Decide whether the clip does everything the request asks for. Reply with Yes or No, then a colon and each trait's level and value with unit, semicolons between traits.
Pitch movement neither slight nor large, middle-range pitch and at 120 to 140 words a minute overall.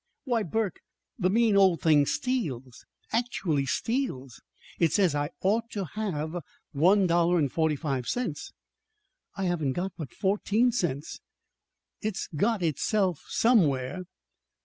No: wide, 6.4 semitones; medium, 180 Hz; slow, 135 wpm